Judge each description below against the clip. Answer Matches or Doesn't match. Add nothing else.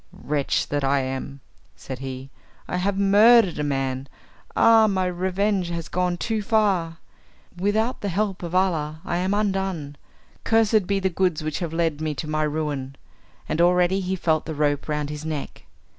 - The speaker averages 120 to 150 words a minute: Doesn't match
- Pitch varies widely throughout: Doesn't match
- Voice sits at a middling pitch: Matches